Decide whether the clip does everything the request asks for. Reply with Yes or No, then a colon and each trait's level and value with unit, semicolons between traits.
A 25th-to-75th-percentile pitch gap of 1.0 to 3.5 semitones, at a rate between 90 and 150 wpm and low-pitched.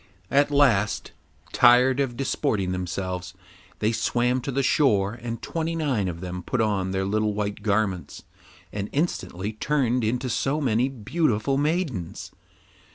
No: wide, 5.5 semitones; average, 140 wpm; low, 115 Hz